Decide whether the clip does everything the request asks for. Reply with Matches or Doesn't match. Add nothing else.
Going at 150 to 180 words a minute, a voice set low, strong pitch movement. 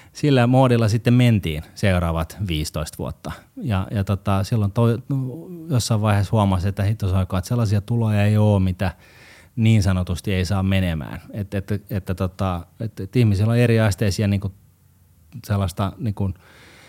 Doesn't match